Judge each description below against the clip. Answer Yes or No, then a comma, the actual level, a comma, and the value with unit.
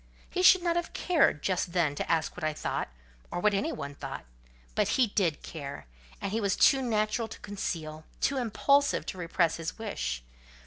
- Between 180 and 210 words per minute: Yes, average, 185 wpm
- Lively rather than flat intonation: Yes, wide, 6.9 semitones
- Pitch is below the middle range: No, high, 190 Hz